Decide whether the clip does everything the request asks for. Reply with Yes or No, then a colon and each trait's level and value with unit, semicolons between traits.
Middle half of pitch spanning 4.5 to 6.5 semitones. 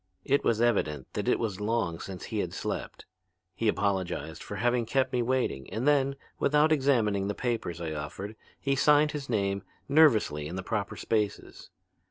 Yes: wide, 5.4 semitones